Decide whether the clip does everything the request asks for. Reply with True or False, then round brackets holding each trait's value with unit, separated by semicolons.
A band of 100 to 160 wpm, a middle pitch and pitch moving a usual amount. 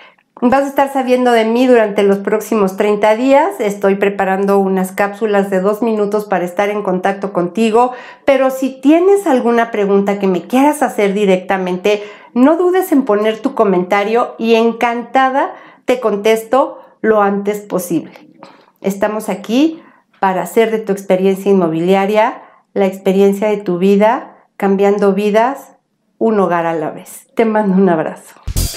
False (145 wpm; 210 Hz; 3.7 semitones)